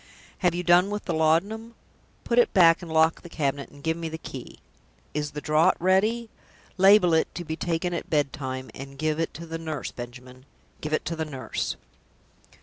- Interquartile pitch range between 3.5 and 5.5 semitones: No, average, 3.1 semitones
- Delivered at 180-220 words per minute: Yes, average, 195 wpm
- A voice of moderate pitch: Yes, medium, 160 Hz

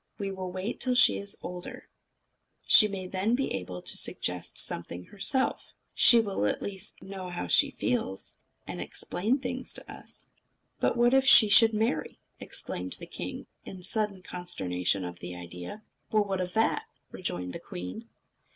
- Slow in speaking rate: No, average, 165 wpm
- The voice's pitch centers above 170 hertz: Yes, high, 190 Hz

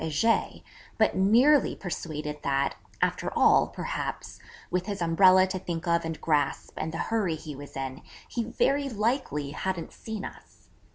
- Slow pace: No, average, 155 wpm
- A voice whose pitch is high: No, medium, 175 Hz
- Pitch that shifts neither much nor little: No, wide, 6.0 semitones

